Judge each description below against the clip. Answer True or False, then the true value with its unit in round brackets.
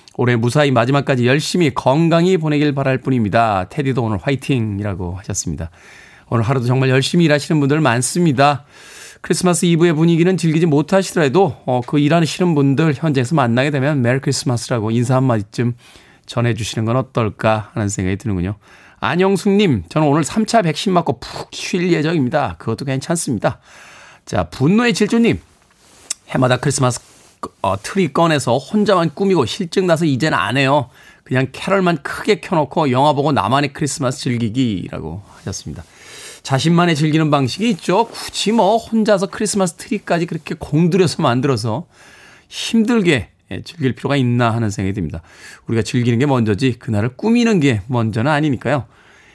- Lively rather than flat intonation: True (6.1 semitones)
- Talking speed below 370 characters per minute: False (375 characters per minute)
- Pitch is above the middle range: False (140 Hz)